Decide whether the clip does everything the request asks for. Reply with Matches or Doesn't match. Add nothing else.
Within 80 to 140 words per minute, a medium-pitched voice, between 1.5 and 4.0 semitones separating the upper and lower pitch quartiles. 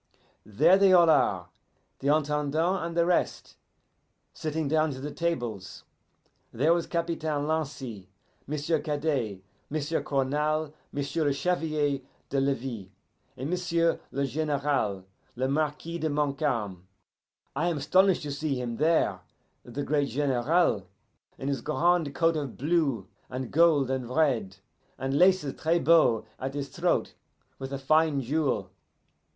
Matches